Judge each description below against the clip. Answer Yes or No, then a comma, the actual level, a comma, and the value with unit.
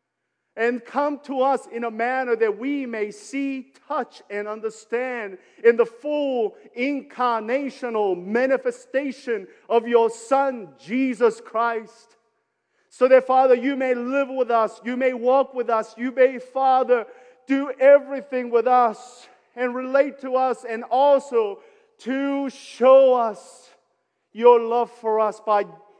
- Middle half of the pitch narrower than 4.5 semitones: Yes, narrow, 2.6 semitones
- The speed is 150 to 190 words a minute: No, slow, 135 wpm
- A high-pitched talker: Yes, very high, 250 Hz